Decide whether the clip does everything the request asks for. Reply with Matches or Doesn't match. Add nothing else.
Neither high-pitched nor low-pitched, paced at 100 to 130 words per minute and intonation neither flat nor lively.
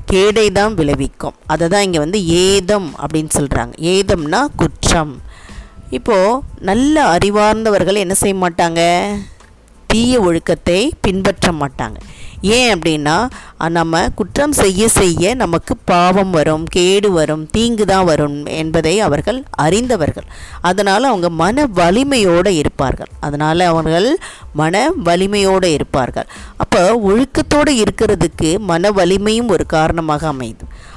Matches